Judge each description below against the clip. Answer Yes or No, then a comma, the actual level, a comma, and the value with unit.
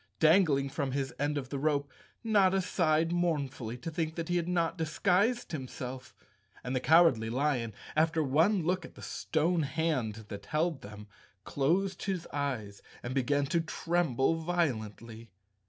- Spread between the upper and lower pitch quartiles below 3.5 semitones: No, average, 4.6 semitones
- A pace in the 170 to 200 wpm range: No, average, 150 wpm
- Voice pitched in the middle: Yes, medium, 155 Hz